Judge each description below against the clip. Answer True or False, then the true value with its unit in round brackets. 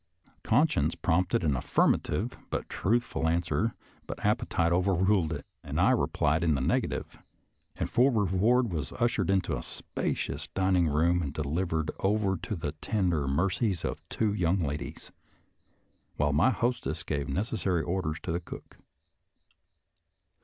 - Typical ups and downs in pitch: True (4.1 semitones)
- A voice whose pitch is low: True (90 Hz)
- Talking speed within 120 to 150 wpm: True (140 wpm)